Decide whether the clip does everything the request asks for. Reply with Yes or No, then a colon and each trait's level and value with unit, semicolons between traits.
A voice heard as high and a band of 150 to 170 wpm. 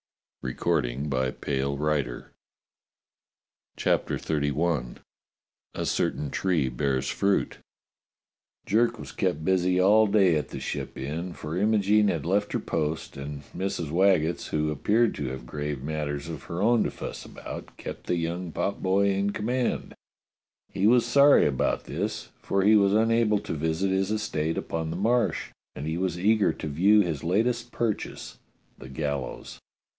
No: very low, 85 Hz; average, 155 wpm